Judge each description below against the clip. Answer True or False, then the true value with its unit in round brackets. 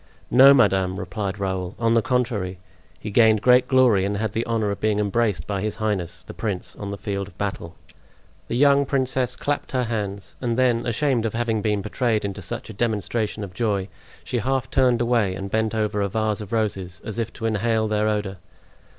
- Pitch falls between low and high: False (110 Hz)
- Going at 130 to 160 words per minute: False (200 wpm)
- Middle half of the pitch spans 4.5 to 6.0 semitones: False (3.0 semitones)